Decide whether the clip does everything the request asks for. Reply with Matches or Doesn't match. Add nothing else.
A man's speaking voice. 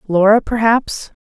Doesn't match